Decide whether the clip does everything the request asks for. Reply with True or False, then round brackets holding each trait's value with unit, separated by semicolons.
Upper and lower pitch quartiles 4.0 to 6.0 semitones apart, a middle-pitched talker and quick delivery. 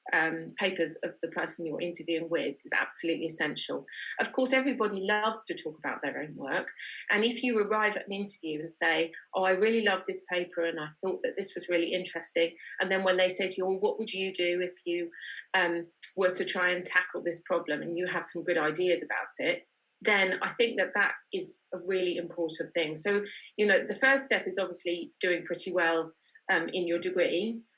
False (2.8 semitones; 180 Hz; 215 wpm)